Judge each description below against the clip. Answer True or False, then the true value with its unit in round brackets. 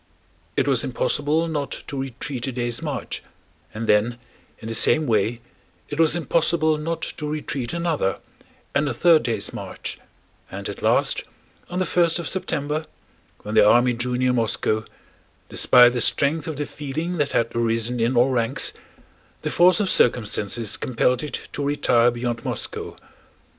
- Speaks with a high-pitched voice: False (130 Hz)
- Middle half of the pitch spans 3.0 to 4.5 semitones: False (4.9 semitones)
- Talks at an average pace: True (155 wpm)